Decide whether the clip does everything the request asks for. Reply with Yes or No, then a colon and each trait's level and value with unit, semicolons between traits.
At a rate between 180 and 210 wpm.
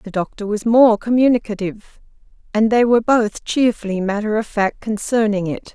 No: average, 155 wpm